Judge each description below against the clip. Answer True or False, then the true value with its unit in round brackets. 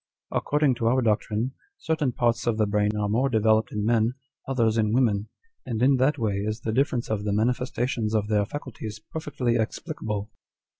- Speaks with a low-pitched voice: True (115 Hz)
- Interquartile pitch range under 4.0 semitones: True (3.1 semitones)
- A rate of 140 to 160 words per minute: False (180 wpm)